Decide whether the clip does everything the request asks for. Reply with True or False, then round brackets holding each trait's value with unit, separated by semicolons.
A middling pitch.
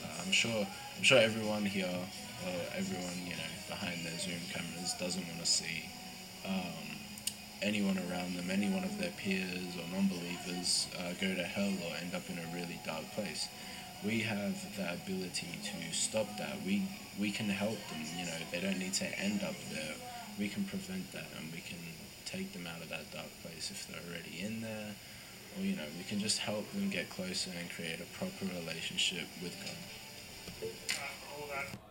False (105 Hz)